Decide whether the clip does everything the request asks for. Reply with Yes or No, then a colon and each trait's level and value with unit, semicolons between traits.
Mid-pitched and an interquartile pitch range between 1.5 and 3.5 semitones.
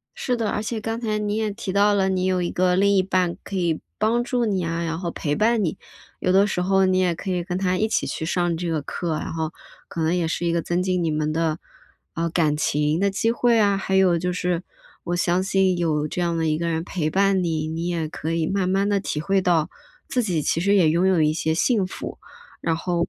Yes: medium, 180 Hz; average, 3.0 semitones